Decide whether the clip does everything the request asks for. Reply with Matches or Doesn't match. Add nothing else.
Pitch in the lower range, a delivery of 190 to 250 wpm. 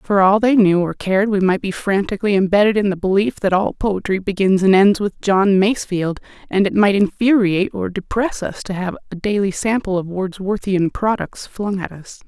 Doesn't match